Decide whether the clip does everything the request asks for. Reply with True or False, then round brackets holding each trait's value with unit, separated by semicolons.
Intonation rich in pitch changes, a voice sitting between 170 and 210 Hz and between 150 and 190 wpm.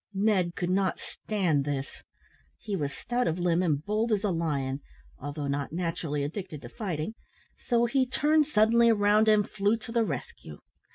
True (6.2 semitones; 190 Hz; 170 wpm)